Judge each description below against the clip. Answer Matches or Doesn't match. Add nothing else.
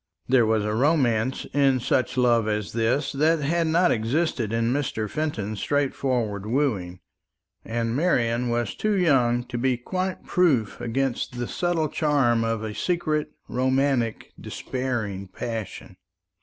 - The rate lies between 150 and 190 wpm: Doesn't match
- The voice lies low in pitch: Matches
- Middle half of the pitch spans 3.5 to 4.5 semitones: Matches